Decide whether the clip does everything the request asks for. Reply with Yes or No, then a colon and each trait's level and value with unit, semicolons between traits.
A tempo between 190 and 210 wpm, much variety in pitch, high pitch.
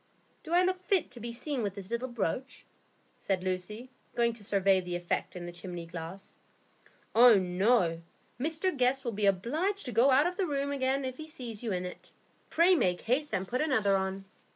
Yes: average, 200 wpm; wide, 6.6 semitones; high, 235 Hz